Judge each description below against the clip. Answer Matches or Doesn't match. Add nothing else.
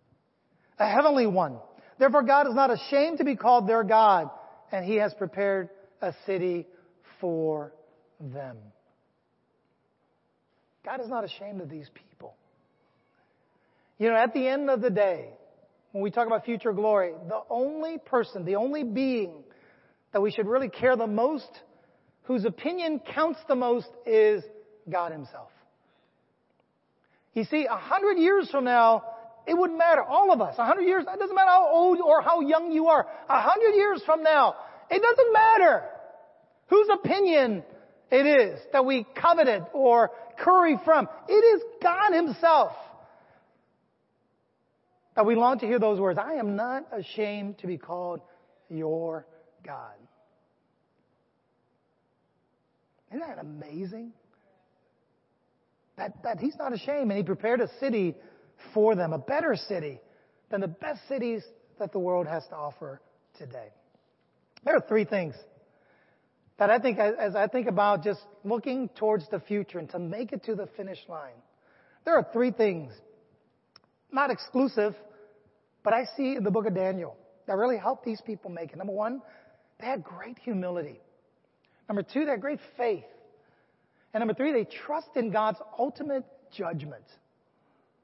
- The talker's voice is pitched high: Matches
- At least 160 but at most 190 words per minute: Doesn't match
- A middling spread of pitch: Doesn't match